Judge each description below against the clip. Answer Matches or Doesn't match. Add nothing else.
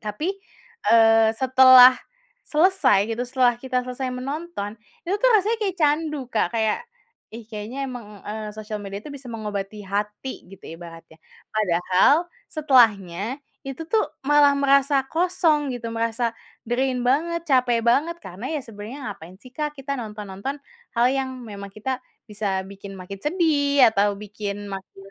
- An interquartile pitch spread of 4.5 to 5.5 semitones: Matches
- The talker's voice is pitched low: Doesn't match